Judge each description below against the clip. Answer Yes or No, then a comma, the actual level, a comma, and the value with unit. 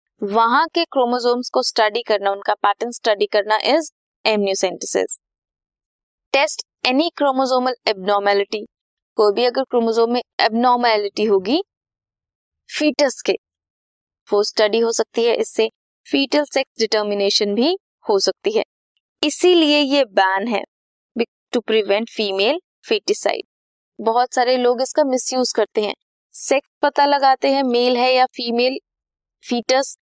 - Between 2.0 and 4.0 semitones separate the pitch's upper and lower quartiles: No, average, 4.4 semitones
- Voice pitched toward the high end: Yes, high, 245 Hz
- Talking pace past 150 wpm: No, average, 120 wpm